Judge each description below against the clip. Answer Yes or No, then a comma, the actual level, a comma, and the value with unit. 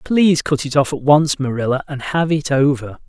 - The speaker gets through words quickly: Yes, fast, 215 wpm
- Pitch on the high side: No, medium, 145 Hz